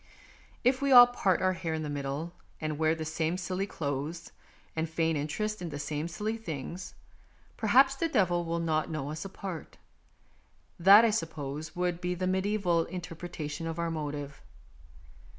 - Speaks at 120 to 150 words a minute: No, average, 165 wpm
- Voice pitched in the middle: Yes, medium, 170 Hz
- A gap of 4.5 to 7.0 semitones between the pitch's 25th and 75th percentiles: No, average, 3.3 semitones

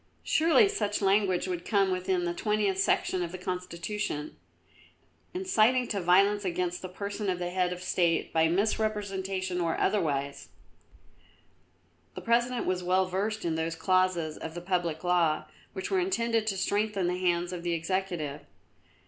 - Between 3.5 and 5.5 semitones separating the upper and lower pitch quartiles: No, average, 2.9 semitones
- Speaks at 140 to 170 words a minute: Yes, average, 155 wpm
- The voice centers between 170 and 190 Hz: Yes, medium, 185 Hz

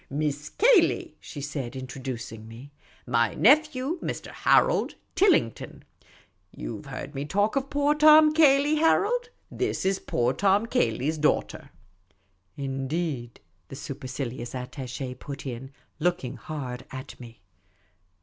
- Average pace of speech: No, slow, 130 wpm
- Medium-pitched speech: Yes, medium, 145 Hz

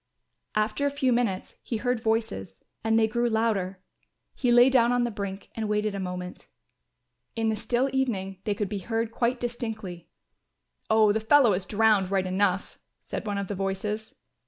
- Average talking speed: Yes, average, 180 wpm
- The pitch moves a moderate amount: Yes, average, 3.3 semitones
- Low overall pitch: No, high, 215 Hz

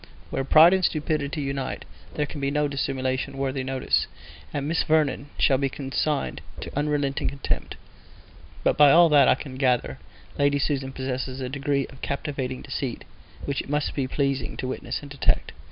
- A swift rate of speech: No, average, 170 wpm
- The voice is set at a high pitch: No, medium, 140 Hz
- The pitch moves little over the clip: Yes, narrow, 1.7 semitones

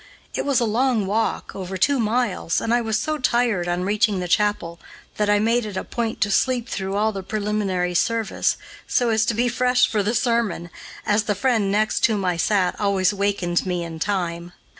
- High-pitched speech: Yes, high, 210 Hz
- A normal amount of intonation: Yes, average, 3.6 semitones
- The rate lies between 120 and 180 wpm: No, fast, 205 wpm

